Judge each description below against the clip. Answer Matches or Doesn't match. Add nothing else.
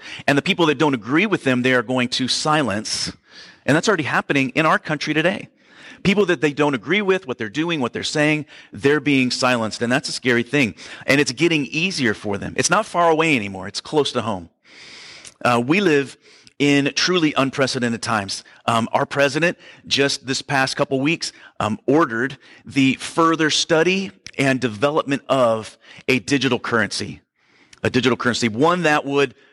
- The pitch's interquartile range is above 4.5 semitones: Doesn't match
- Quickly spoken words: Doesn't match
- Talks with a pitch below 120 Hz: Doesn't match